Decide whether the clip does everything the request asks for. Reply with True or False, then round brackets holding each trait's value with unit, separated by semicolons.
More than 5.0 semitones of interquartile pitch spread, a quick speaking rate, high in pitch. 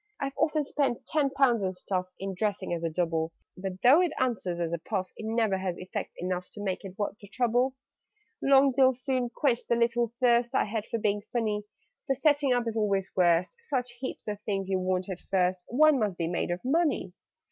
True (5.5 semitones; 210 wpm; 215 Hz)